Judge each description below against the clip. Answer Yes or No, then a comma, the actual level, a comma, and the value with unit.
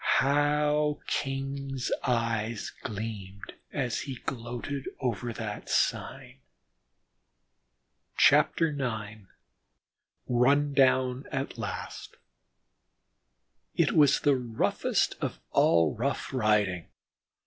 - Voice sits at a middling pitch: No, low, 125 Hz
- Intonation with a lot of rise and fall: No, average, 3.8 semitones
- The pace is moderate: No, slow, 80 wpm